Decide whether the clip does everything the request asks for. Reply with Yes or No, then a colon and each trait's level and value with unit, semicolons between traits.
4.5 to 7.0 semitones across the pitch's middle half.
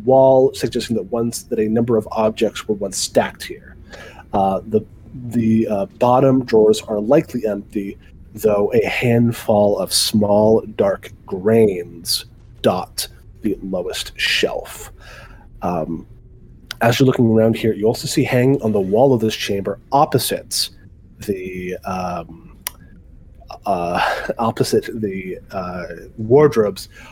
No: average, 3.7 semitones